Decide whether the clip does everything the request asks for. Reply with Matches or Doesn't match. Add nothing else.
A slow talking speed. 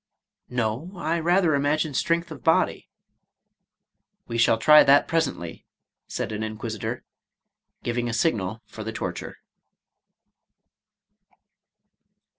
Matches